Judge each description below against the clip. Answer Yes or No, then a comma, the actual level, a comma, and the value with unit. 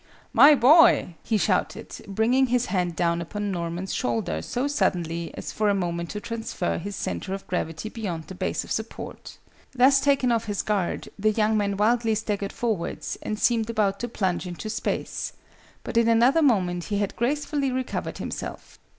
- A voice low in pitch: No, high, 210 Hz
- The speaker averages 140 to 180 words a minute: Yes, average, 175 wpm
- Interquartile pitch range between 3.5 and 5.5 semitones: Yes, average, 4.8 semitones